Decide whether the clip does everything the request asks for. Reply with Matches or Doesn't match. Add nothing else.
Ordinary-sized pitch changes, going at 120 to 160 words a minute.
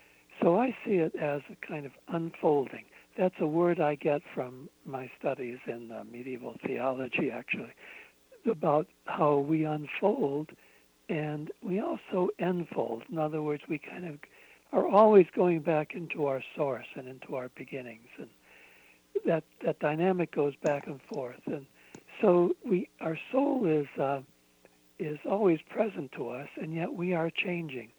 Matches